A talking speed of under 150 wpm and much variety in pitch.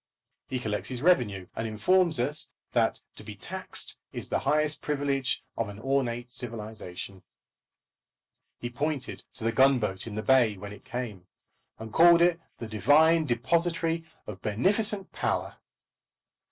Yes: average, 140 wpm; wide, 6.2 semitones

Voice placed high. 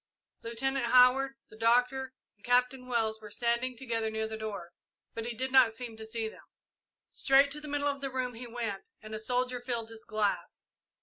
Yes: high, 240 Hz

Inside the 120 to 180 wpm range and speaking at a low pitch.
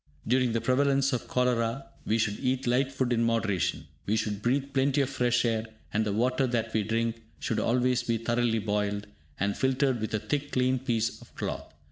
No: average, 195 wpm; low, 120 Hz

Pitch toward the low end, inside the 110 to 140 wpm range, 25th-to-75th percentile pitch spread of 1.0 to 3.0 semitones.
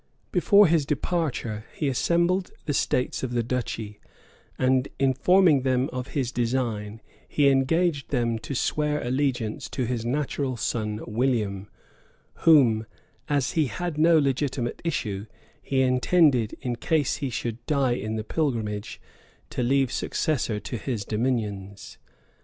No: low, 130 Hz; slow, 135 wpm; average, 4.2 semitones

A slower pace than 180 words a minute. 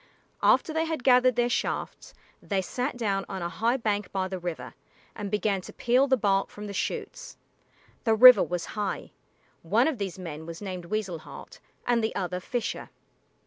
No: average, 185 wpm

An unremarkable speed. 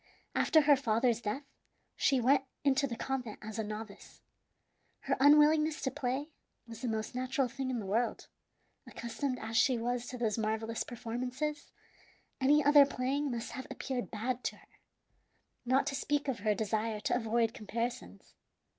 Yes: average, 160 wpm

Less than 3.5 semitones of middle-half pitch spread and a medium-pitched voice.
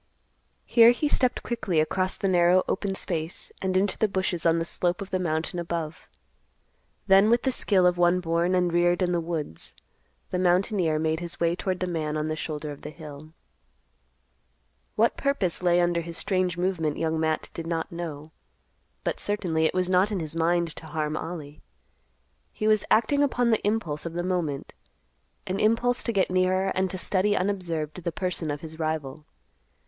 Yes: average, 2.8 semitones; medium, 175 Hz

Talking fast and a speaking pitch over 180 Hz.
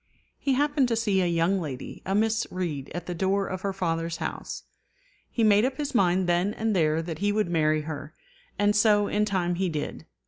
Yes: fast, 210 wpm; high, 190 Hz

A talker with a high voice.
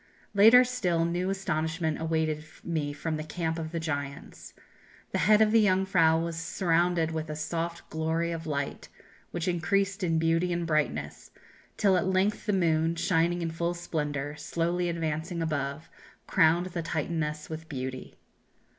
No: medium, 165 Hz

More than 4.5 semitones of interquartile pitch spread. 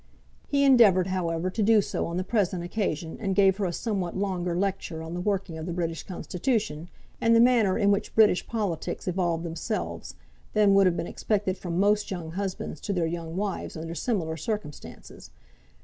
No: average, 3.5 semitones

